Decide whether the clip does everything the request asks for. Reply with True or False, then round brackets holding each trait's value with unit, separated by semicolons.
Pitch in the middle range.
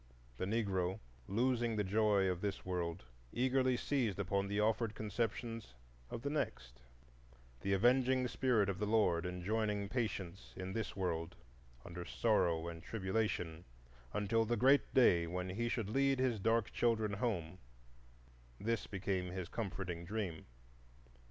False (100 Hz)